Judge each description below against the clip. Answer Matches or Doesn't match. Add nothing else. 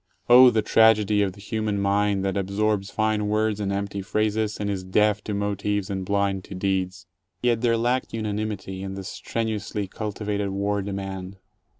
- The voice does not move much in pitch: Matches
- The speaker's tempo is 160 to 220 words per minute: Matches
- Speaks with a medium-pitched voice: Doesn't match